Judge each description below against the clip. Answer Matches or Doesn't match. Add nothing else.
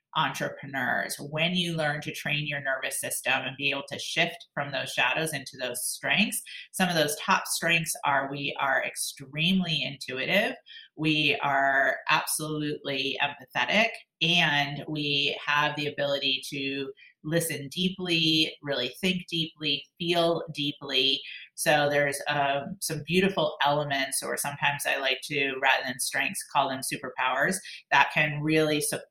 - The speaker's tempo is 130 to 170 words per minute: Matches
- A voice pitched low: Doesn't match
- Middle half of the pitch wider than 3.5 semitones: Doesn't match